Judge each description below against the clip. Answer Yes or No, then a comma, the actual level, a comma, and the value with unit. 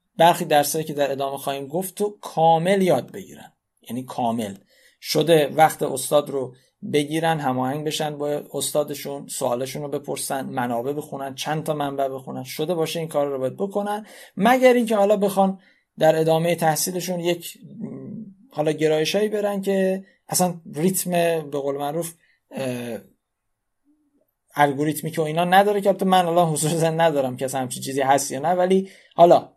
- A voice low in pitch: No, medium, 160 Hz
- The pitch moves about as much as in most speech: Yes, average, 4.7 semitones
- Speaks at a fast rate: No, average, 145 wpm